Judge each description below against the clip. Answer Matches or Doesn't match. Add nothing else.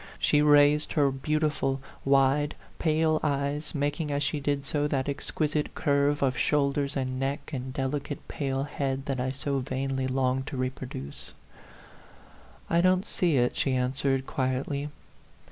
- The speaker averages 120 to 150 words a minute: Matches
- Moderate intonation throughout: Doesn't match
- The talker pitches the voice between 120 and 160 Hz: Matches